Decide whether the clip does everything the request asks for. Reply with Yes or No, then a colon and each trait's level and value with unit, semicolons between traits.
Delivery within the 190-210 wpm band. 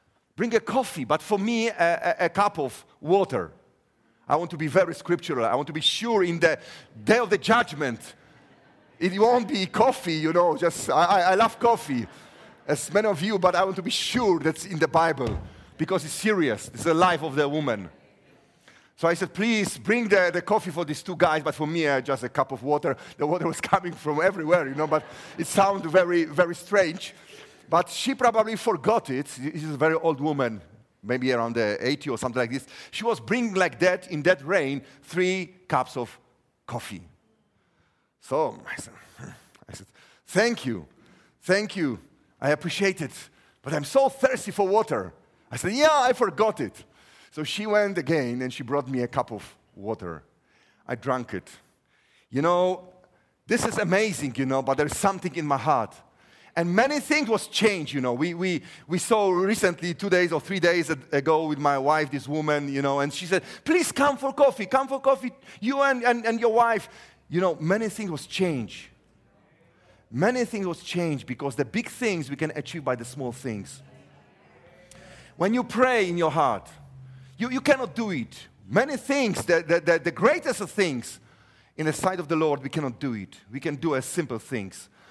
Yes: average, 195 wpm